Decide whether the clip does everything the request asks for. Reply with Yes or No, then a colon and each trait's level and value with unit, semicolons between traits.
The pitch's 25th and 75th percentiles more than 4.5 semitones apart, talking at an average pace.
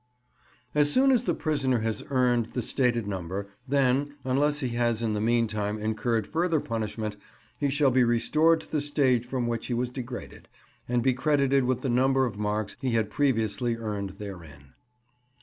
No: average, 4.0 semitones; average, 175 wpm